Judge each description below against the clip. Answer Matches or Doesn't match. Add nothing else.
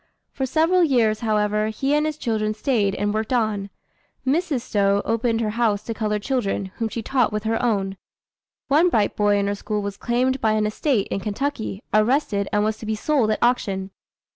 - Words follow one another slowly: Doesn't match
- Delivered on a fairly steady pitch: Doesn't match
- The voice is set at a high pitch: Matches